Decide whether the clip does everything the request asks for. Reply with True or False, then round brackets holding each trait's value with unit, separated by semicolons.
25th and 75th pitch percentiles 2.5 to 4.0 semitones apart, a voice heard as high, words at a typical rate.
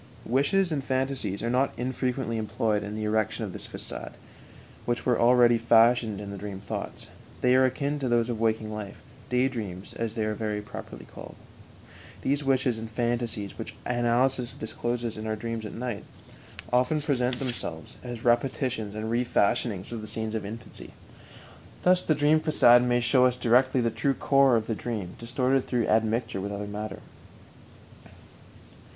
False (2.8 semitones; 120 Hz; 170 wpm)